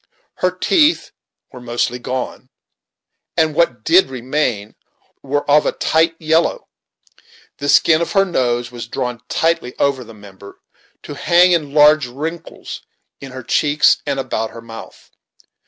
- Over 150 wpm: No, average, 140 wpm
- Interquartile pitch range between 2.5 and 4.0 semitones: No, average, 4.9 semitones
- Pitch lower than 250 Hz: Yes, medium, 140 Hz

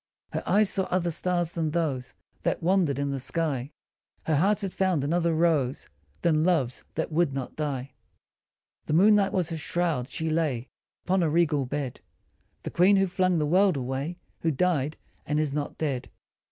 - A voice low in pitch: No, medium, 160 Hz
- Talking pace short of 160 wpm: No, average, 175 wpm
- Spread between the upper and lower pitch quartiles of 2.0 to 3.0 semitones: No, average, 4.0 semitones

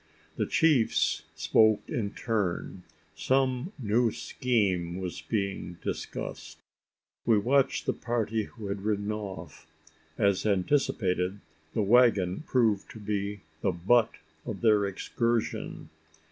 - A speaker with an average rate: No, slow, 115 wpm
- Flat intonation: No, average, 3.3 semitones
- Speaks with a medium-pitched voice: No, low, 105 Hz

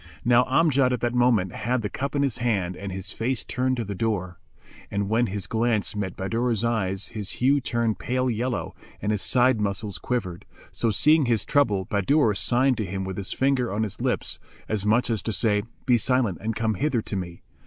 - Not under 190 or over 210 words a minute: Yes, fast, 205 wpm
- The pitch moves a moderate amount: Yes, average, 3.8 semitones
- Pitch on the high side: No, low, 115 Hz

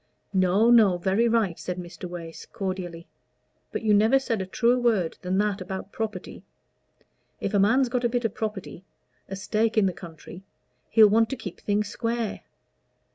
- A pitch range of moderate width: Yes, average, 3.6 semitones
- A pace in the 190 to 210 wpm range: No, average, 175 wpm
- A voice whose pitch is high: Yes, high, 205 Hz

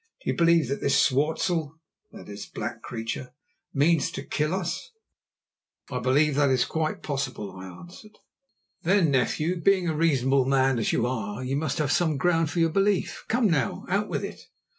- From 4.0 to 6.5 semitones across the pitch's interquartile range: Yes, average, 4.4 semitones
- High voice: No, medium, 150 Hz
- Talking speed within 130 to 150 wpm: No, average, 185 wpm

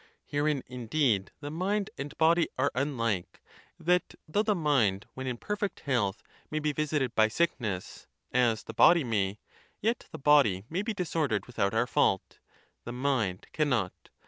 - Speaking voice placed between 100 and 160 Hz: Yes, low, 135 Hz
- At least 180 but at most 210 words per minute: No, average, 165 wpm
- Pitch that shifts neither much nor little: No, wide, 5.9 semitones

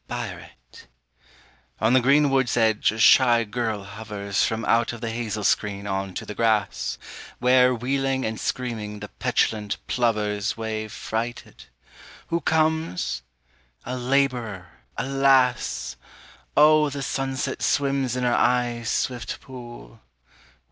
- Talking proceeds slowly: Yes, slow, 125 wpm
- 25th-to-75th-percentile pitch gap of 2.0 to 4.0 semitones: Yes, average, 3.5 semitones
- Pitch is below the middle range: Yes, low, 120 Hz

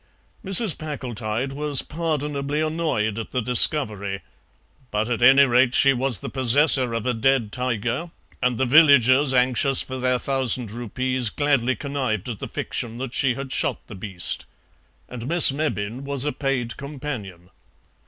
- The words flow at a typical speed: Yes, average, 155 wpm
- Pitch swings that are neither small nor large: Yes, average, 3.3 semitones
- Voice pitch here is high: No, low, 130 Hz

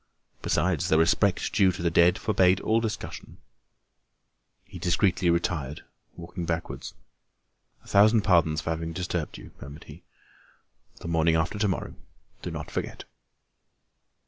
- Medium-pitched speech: No, very low, 85 Hz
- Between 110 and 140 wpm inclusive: Yes, slow, 135 wpm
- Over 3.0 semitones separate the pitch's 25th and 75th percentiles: No, narrow, 2.4 semitones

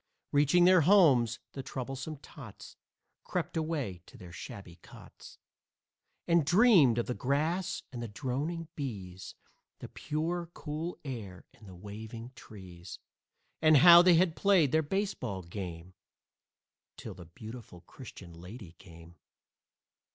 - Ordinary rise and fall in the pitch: No, wide, 8.8 semitones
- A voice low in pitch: Yes, low, 130 Hz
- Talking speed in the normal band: No, slow, 130 wpm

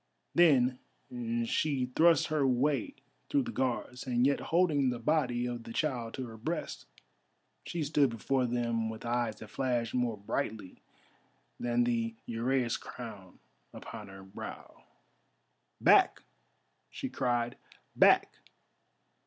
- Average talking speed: No, slow, 125 wpm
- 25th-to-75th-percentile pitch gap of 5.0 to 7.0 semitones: No, average, 3.0 semitones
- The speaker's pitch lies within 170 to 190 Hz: No, low, 125 Hz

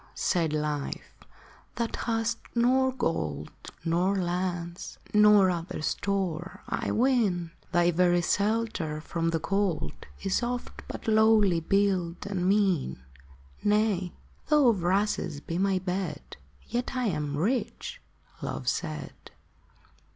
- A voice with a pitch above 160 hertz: Yes, medium, 185 Hz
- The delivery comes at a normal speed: No, slow, 120 wpm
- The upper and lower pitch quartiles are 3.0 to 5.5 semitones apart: Yes, average, 4.2 semitones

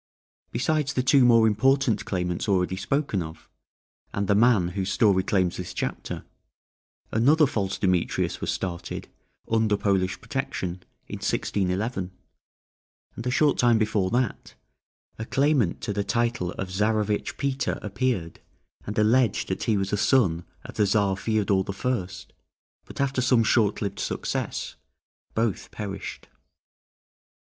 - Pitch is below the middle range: Yes, low, 105 Hz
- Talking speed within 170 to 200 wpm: No, average, 140 wpm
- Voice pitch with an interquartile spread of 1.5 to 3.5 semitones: No, average, 4.2 semitones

